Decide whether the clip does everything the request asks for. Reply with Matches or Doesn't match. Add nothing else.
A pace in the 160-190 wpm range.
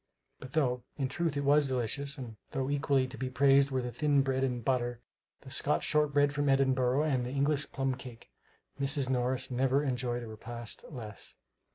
Matches